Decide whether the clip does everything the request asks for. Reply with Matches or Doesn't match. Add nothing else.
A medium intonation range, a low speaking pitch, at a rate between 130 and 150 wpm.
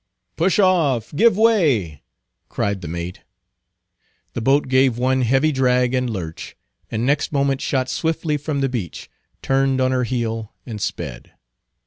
Matches